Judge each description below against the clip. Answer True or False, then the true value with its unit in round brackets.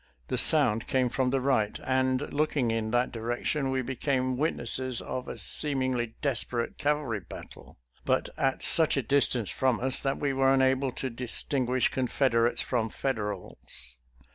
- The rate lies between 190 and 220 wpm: False (155 wpm)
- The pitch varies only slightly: True (2.2 semitones)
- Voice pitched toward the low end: True (130 Hz)